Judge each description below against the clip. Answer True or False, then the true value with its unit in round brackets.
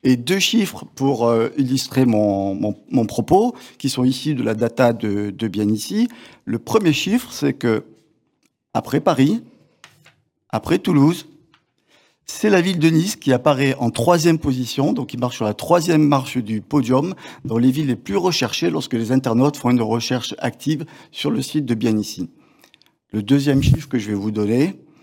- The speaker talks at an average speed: True (175 wpm)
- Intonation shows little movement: False (4.8 semitones)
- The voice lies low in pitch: True (130 Hz)